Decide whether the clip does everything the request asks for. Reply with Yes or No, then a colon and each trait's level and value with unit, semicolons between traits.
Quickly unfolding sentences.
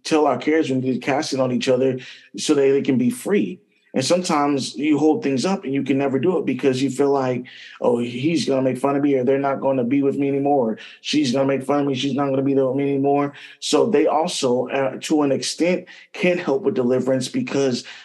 Yes: fast, 265 wpm